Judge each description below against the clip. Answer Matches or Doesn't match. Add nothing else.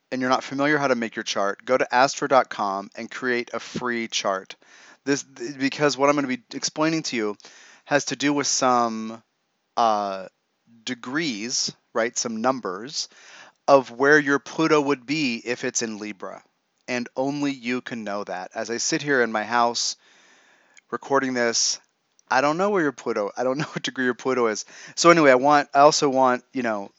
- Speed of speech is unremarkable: Matches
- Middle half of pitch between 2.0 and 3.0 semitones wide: Doesn't match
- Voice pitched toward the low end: Matches